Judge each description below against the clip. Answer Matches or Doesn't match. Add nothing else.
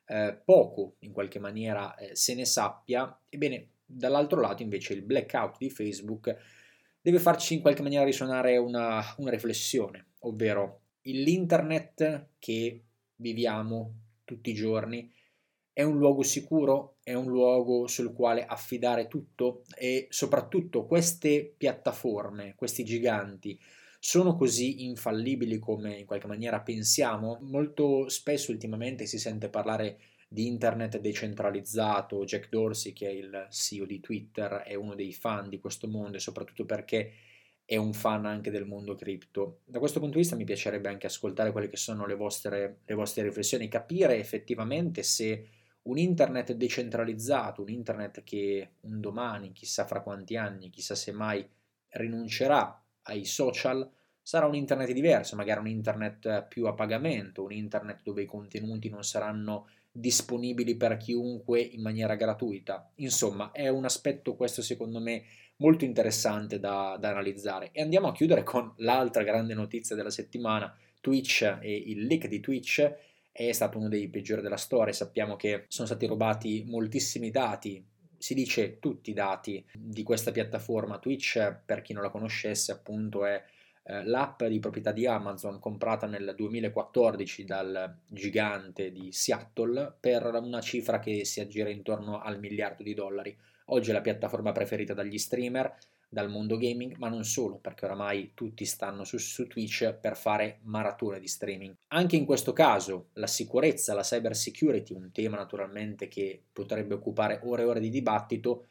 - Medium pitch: Doesn't match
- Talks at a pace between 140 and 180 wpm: Matches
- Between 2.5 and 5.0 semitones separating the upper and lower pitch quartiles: Matches